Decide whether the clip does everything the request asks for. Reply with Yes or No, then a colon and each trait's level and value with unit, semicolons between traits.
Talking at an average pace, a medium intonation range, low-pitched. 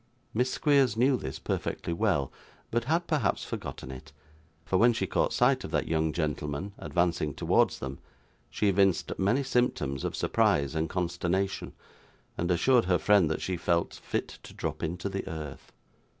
No: average, 165 wpm; wide, 5.8 semitones; very low, 90 Hz